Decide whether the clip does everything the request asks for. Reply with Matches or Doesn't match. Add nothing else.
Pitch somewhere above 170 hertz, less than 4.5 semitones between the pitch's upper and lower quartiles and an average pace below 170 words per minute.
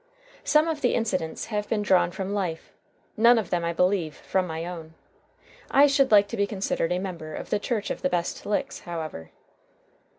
Doesn't match